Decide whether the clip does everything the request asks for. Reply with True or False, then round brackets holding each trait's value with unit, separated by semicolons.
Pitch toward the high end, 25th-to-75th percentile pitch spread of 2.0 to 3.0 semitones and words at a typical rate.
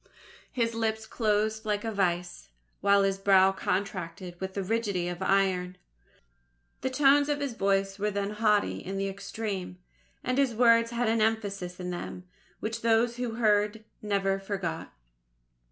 True (205 Hz; 2.7 semitones; 155 wpm)